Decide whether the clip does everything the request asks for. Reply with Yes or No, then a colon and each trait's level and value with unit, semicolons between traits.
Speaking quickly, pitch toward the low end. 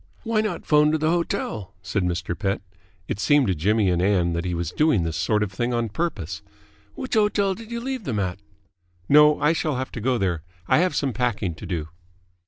Yes: fast, 215 wpm; low, 115 Hz